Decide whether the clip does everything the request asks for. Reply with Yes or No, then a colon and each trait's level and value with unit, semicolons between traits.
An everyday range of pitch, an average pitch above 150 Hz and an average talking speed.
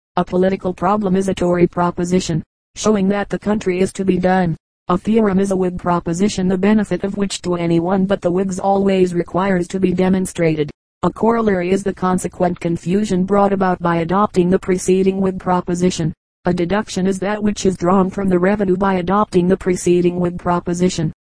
No: narrow, 1.5 semitones; medium, 185 Hz; average, 185 wpm